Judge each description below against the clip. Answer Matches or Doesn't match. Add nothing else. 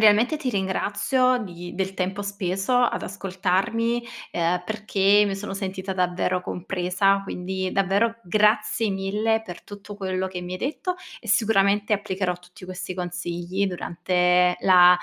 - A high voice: Matches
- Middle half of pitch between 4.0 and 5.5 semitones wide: Doesn't match